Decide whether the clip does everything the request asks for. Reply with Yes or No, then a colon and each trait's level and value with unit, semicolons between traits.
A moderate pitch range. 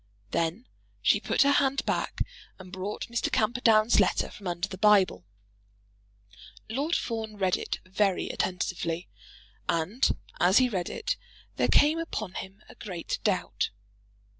Yes: average, 4.4 semitones